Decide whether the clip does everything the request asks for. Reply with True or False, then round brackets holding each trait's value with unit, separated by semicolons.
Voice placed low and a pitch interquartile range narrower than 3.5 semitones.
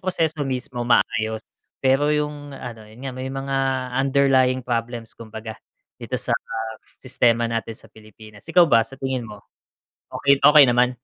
True (125 Hz; 3.1 semitones)